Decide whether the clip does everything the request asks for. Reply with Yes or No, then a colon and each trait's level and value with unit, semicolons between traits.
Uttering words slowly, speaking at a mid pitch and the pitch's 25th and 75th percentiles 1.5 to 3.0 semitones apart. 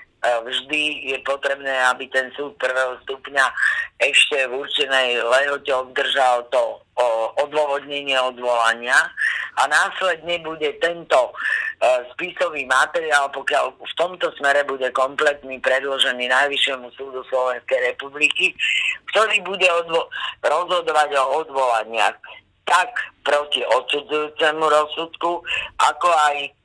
No: slow, 105 wpm; medium, 145 Hz; average, 3.9 semitones